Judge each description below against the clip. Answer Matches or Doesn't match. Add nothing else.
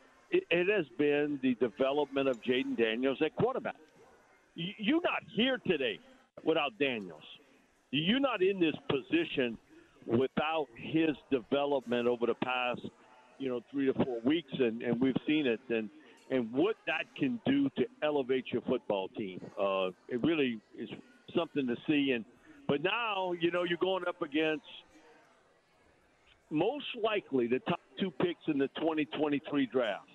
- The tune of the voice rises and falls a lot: Matches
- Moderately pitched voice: Matches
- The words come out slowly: Doesn't match